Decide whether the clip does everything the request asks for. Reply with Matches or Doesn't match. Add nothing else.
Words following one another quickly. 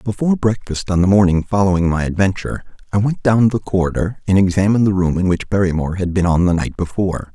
Matches